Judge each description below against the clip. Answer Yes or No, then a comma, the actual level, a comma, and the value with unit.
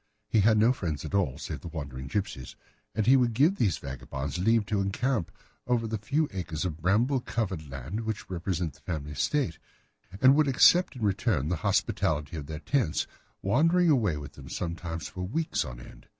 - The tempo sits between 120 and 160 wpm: No, average, 190 wpm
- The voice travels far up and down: Yes, wide, 7.5 semitones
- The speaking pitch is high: No, very low, 95 Hz